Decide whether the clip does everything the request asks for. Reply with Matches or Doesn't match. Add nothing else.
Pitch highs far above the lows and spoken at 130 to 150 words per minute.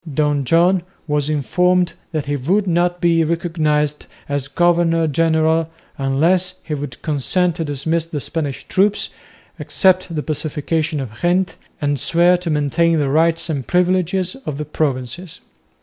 Doesn't match